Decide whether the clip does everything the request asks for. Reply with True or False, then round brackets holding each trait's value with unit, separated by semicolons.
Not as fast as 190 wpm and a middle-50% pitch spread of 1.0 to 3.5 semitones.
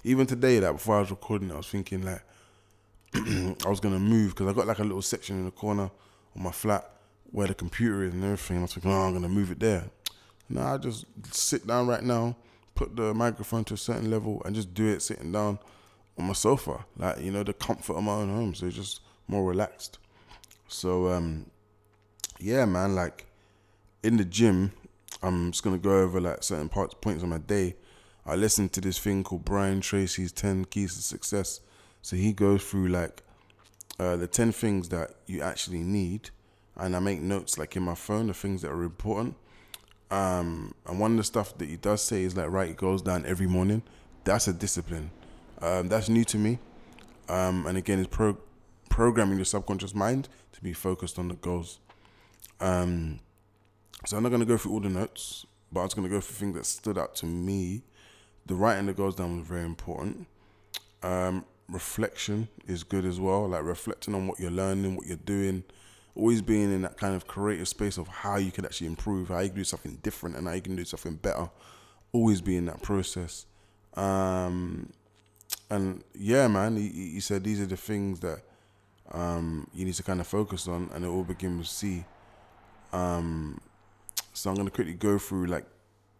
False (205 wpm; 2.5 semitones)